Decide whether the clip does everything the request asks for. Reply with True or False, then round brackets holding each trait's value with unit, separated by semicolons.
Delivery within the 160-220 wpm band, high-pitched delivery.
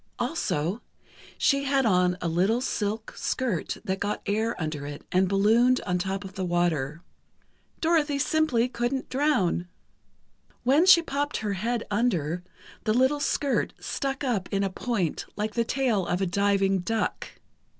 False (150 wpm; 210 Hz)